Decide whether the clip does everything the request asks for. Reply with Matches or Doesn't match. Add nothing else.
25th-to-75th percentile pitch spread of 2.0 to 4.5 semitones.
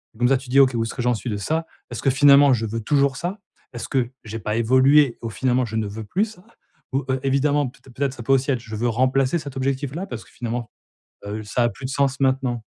Matches